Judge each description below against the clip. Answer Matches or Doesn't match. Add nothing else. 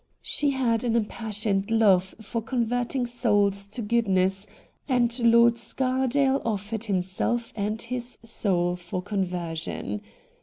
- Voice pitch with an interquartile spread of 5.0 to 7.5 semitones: Doesn't match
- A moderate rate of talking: Doesn't match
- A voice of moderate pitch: Doesn't match